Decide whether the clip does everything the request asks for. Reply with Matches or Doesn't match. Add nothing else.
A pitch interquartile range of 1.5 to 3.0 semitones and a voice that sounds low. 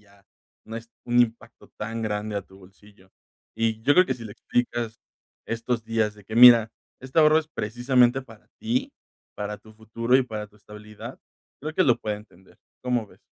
Matches